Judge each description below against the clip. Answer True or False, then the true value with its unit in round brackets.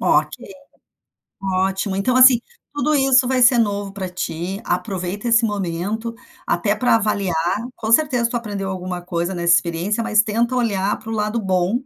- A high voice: True (210 Hz)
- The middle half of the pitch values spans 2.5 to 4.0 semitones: True (3.7 semitones)